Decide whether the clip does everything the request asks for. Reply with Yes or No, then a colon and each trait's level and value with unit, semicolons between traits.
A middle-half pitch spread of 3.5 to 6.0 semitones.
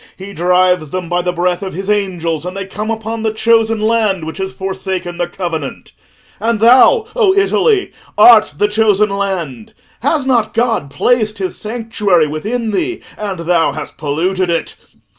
Yes: average, 4.2 semitones